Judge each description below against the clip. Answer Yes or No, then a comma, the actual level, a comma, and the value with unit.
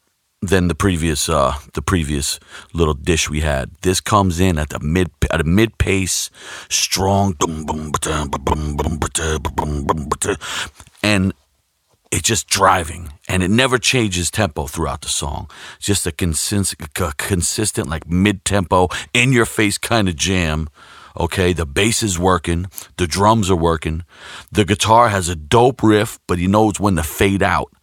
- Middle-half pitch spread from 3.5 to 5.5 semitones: Yes, average, 3.9 semitones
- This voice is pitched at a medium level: No, very low, 90 Hz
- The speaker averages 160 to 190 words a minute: No, average, 150 wpm